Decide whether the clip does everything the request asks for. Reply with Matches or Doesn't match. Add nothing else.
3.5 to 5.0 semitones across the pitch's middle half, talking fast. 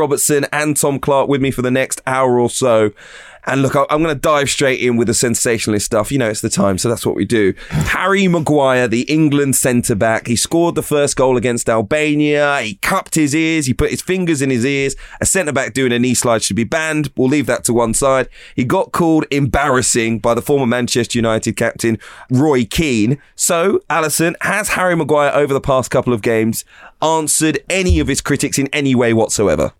Matches